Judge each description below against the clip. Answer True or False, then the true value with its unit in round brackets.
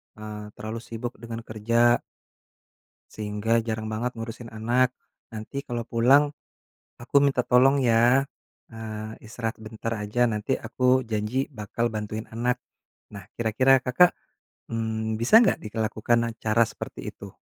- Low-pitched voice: True (115 Hz)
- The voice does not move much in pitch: True (2.1 semitones)